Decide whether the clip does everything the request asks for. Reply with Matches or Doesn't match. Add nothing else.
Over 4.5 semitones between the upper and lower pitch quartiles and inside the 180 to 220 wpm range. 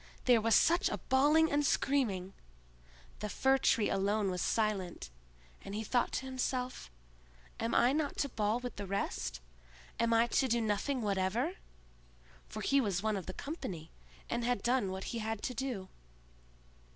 Doesn't match